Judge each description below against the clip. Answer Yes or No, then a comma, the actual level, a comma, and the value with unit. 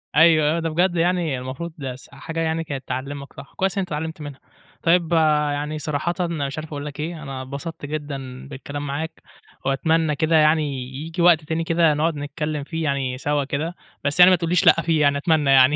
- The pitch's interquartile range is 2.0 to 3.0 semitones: Yes, narrow, 2.6 semitones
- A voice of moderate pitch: Yes, medium, 150 Hz